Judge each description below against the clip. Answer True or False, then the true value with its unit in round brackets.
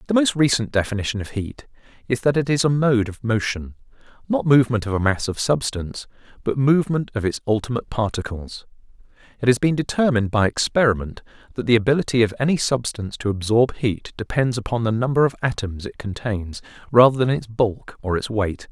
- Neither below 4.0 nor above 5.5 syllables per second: False (5.9 syllables/s)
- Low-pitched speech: True (120 Hz)